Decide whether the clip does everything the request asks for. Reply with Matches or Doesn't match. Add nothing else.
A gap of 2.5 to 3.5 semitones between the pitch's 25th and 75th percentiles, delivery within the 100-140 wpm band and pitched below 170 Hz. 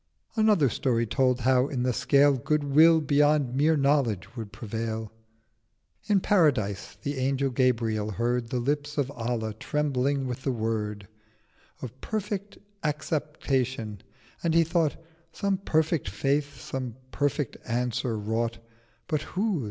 Doesn't match